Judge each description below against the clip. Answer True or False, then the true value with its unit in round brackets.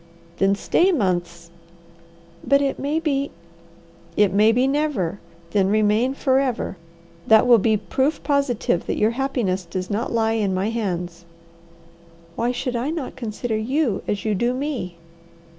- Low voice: False (225 Hz)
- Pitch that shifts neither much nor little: False (5.7 semitones)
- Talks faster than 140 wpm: True (150 wpm)